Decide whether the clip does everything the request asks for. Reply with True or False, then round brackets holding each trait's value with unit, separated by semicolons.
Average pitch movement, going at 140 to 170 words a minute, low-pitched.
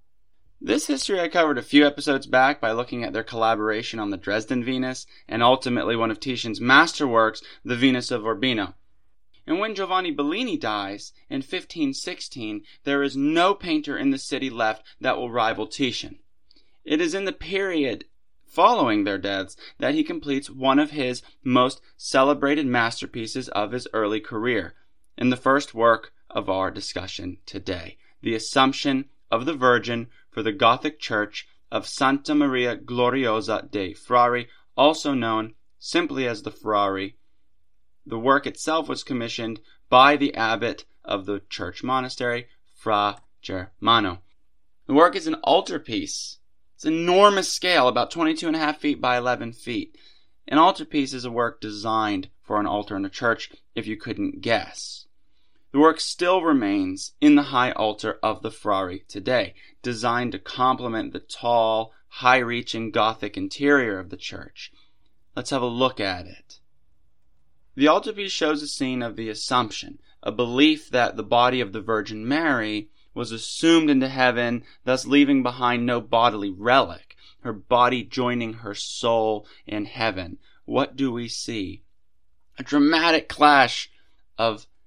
True (4.8 semitones; 150 wpm; 125 Hz)